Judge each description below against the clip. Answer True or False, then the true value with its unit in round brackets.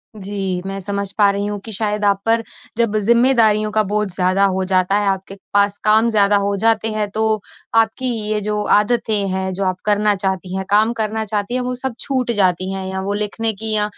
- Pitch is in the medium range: False (205 Hz)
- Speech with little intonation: True (2.0 semitones)